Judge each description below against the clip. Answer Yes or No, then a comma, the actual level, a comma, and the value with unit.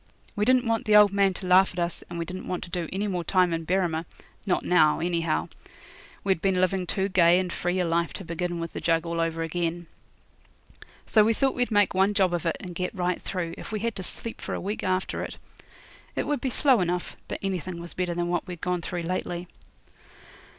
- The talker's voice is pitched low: No, medium, 180 Hz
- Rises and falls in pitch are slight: Yes, narrow, 2.3 semitones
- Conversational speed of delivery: No, fast, 230 wpm